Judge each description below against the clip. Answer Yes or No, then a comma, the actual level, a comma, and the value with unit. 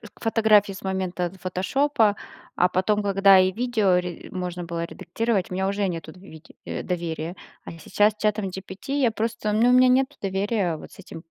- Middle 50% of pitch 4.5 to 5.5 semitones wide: No, average, 3.2 semitones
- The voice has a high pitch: Yes, high, 195 Hz